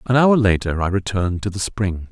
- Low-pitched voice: Yes, low, 100 Hz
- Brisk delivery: Yes, fast, 225 wpm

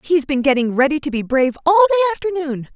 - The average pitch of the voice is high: Yes, very high, 305 Hz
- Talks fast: Yes, fast, 220 wpm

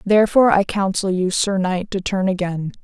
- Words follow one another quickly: No, average, 190 wpm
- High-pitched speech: Yes, high, 195 Hz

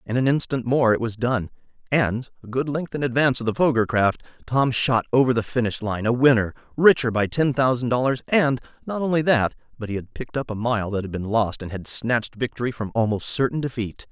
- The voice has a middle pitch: No, low, 120 Hz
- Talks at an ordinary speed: No, fast, 225 wpm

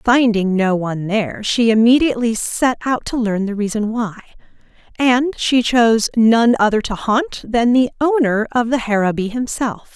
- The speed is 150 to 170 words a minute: Yes, average, 165 wpm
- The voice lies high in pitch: Yes, high, 230 Hz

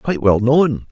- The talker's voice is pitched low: Yes, low, 130 Hz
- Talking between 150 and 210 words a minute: Yes, average, 200 wpm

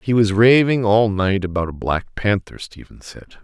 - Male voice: Yes, male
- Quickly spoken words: No, average, 190 wpm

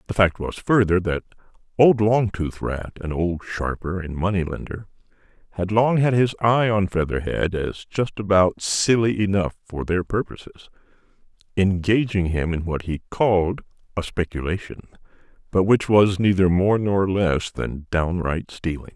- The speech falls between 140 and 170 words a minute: Yes, average, 145 wpm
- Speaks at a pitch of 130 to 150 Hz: No, very low, 95 Hz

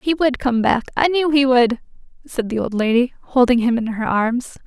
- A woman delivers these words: Yes, female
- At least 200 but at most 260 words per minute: Yes, fast, 205 wpm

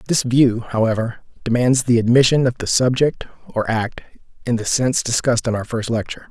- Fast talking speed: No, average, 180 wpm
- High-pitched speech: No, low, 120 Hz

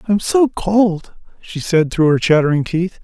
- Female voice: No, male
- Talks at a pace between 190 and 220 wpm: No, average, 180 wpm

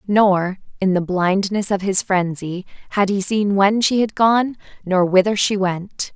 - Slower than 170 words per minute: No, average, 175 wpm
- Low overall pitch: No, high, 195 Hz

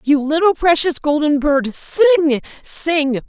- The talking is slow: Yes, slow, 130 wpm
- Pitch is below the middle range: No, very high, 305 Hz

